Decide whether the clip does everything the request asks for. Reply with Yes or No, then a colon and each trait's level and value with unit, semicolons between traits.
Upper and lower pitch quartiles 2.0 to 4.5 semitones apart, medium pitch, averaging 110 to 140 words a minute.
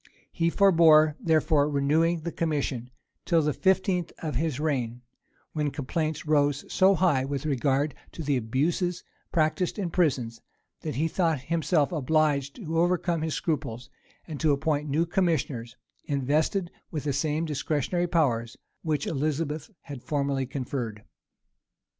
Yes: average, 3.1 semitones; medium, 155 Hz; slow, 135 wpm